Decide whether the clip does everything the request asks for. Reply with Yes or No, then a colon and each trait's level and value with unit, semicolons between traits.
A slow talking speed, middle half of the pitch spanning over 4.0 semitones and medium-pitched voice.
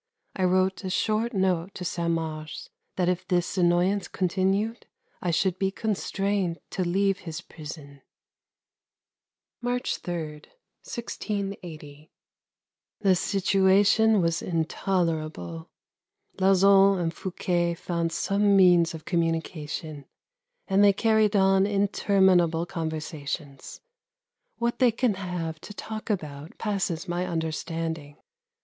No: slow, 110 wpm; average, 3.2 semitones; medium, 180 Hz